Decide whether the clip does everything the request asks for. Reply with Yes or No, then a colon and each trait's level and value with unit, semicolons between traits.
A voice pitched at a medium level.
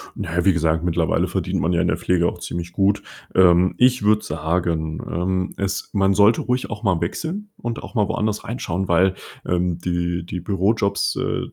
No: very low, 90 Hz